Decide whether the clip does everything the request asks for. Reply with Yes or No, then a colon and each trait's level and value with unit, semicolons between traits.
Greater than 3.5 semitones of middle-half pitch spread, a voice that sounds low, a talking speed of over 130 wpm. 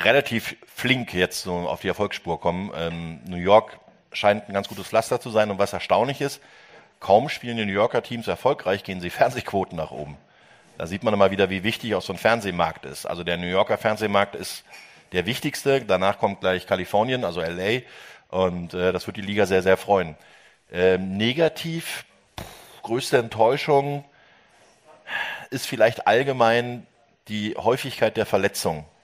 Yes: average, 4.1 semitones; low, 100 Hz; average, 165 wpm